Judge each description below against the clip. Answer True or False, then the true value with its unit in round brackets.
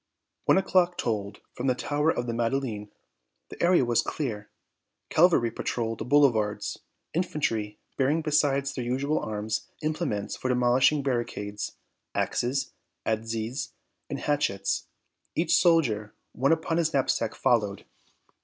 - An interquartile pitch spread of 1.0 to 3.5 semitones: False (5.1 semitones)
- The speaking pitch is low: True (125 Hz)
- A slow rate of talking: True (125 wpm)